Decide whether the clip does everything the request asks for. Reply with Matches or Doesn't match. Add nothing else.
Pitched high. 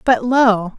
Matches